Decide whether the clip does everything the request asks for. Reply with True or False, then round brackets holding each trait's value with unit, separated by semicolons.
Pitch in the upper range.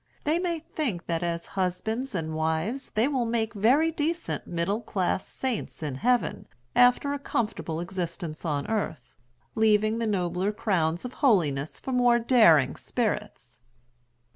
True (210 Hz)